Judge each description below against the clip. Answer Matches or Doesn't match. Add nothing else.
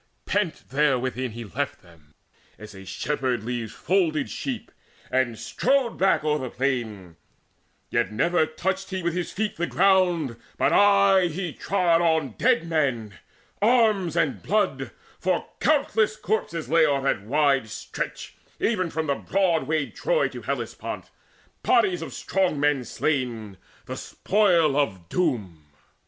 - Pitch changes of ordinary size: Doesn't match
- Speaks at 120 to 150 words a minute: Matches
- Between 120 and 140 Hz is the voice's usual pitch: Doesn't match